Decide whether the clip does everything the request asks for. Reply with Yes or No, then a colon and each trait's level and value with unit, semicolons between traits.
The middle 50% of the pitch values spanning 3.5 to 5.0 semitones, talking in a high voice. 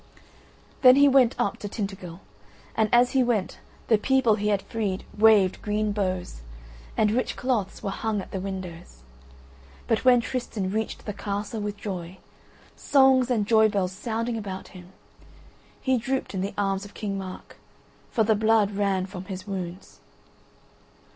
No: average, 2.9 semitones; high, 205 Hz